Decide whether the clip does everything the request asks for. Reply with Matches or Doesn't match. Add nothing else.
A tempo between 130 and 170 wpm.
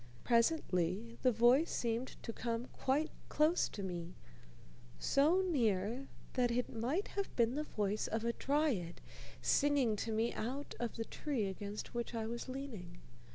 Matches